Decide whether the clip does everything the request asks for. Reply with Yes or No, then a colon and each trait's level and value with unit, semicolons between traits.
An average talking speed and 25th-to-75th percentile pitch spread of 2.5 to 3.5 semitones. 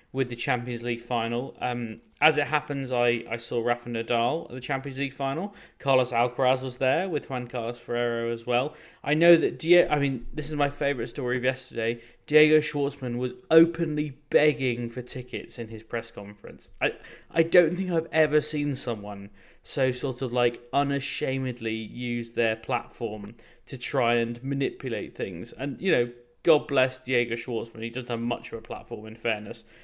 Yes: average, 180 wpm; average, 3.2 semitones